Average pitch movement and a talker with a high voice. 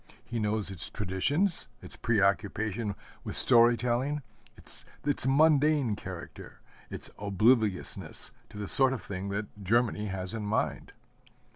No: average, 4.2 semitones; low, 110 Hz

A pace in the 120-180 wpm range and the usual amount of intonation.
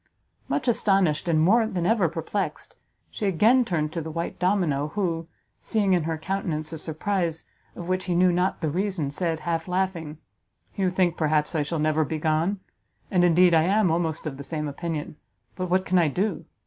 No: average, 190 wpm; average, 3.1 semitones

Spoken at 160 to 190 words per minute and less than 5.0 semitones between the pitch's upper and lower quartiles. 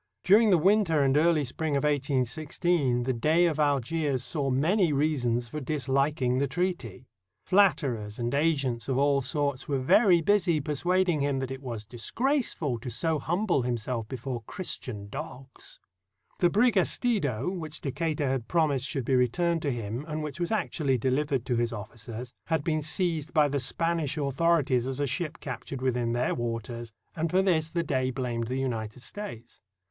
Yes: average, 170 wpm; average, 4.6 semitones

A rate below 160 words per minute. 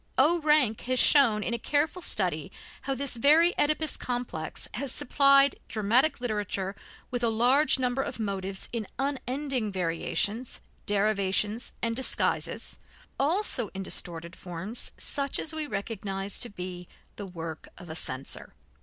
Yes: average, 140 wpm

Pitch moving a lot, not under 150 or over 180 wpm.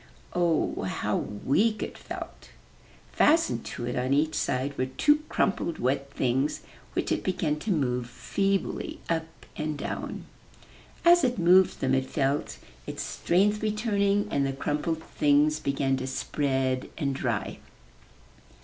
No: wide, 6.3 semitones; average, 140 wpm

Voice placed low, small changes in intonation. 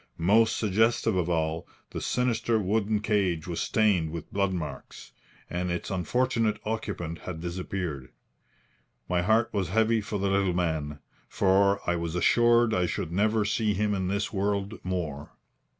No: low, 100 Hz; average, 3.8 semitones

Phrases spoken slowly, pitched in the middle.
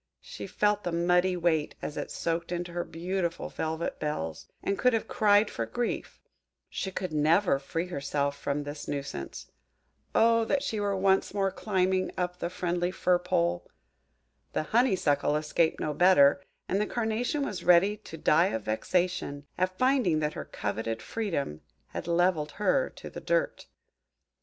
No: average, 160 wpm; medium, 175 Hz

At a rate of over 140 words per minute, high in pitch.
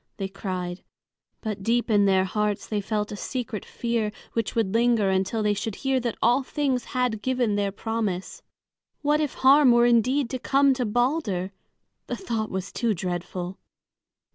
Yes: average, 165 wpm; high, 225 Hz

